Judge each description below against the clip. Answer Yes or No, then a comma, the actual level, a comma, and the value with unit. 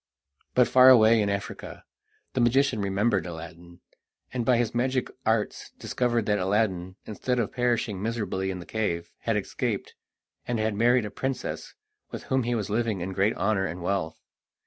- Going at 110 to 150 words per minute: No, average, 170 wpm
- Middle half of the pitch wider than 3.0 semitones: Yes, average, 4.0 semitones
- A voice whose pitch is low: Yes, low, 110 Hz